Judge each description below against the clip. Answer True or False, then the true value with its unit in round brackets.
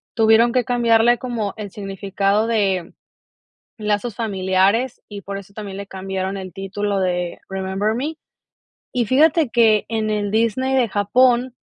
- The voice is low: False (210 Hz)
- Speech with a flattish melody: False (3.3 semitones)